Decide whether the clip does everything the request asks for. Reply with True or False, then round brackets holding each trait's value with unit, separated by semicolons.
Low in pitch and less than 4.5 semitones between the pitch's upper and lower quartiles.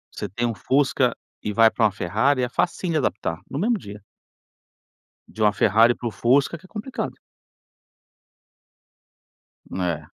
False (120 Hz; 5.4 semitones)